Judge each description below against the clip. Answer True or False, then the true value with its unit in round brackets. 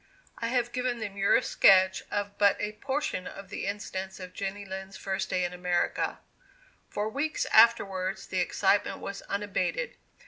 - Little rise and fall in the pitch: True (2.2 semitones)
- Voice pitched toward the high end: True (200 Hz)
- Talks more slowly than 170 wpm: True (160 wpm)